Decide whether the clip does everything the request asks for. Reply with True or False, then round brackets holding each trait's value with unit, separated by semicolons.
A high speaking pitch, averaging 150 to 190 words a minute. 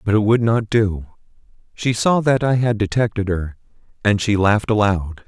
False (105 Hz; 180 wpm)